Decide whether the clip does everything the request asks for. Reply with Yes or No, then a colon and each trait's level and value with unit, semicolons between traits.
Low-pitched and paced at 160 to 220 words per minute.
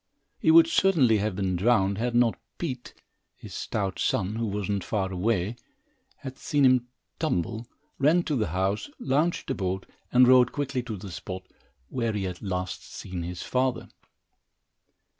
Yes: low, 110 Hz; average, 165 wpm